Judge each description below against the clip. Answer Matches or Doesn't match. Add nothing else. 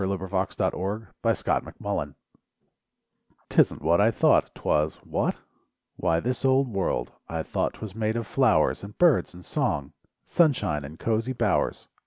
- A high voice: Doesn't match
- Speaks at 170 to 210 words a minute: Doesn't match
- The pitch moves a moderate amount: Doesn't match